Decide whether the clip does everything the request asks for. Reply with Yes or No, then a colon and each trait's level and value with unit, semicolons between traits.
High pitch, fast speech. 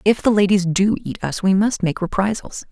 Yes: high, 195 Hz; fast, 220 wpm